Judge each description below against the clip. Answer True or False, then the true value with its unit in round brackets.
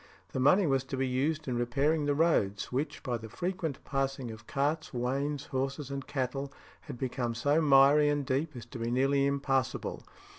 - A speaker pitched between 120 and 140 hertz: True (135 Hz)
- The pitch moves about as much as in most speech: False (2.3 semitones)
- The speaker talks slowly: False (185 wpm)